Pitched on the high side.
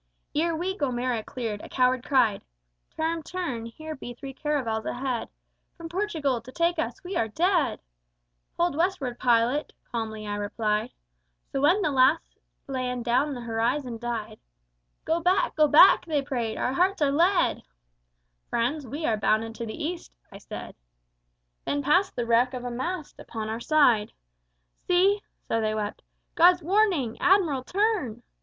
Yes: very high, 270 Hz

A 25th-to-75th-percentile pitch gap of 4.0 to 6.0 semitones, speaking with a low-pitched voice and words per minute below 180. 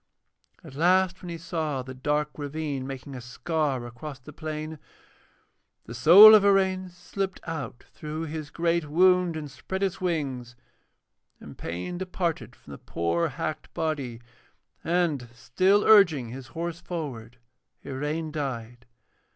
No: average, 5.1 semitones; medium, 155 Hz; slow, 135 wpm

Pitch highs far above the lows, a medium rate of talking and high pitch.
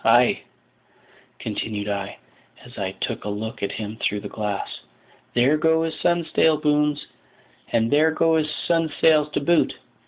No: wide, 6.8 semitones; average, 150 wpm; medium, 150 Hz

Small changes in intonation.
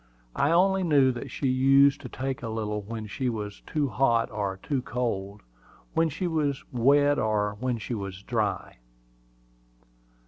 No: average, 4.9 semitones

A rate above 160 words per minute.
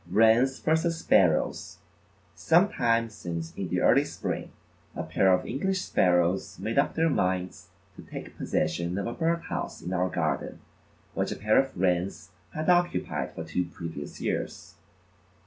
No: average, 155 wpm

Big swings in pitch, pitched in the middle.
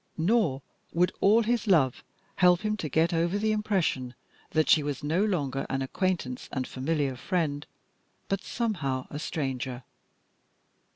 Yes: wide, 6.3 semitones; medium, 160 Hz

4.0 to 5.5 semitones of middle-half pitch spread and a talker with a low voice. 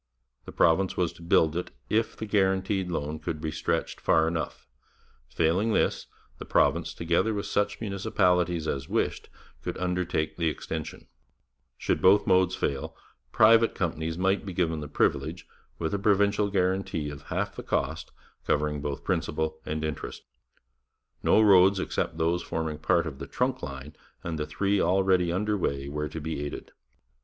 No: average, 3.6 semitones; very low, 85 Hz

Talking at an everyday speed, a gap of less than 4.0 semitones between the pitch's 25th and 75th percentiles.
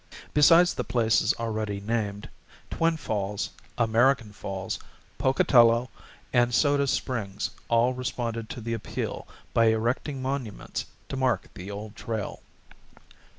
No: slow, 115 wpm; average, 3.2 semitones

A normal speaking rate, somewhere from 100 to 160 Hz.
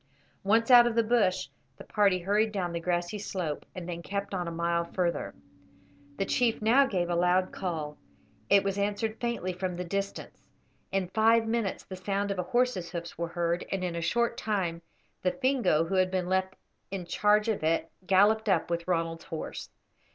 No: average, 190 wpm; high, 190 Hz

